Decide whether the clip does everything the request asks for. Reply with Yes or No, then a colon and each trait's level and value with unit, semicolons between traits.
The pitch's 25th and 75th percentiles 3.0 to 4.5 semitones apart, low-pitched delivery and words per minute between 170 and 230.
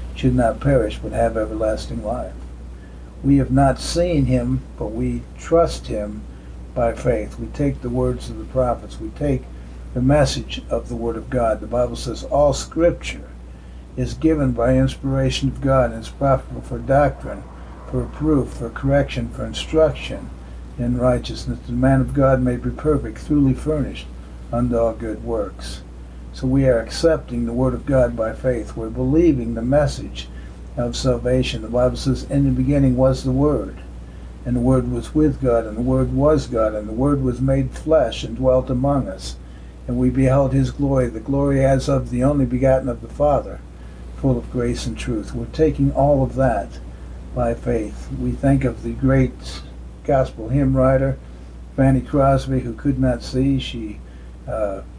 Yes: average, 4.0 semitones; low, 125 Hz; average, 175 wpm